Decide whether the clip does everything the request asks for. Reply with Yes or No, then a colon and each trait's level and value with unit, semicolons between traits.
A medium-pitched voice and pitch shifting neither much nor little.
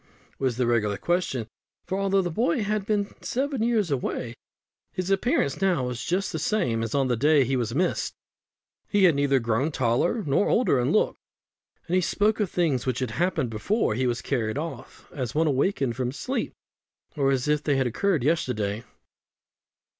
No: medium, 145 Hz; wide, 7.5 semitones